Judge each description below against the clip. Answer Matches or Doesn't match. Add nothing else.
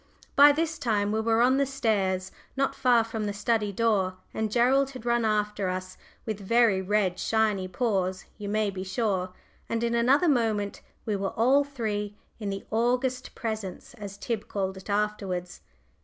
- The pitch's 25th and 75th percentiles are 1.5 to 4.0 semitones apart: Matches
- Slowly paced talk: Doesn't match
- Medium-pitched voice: Doesn't match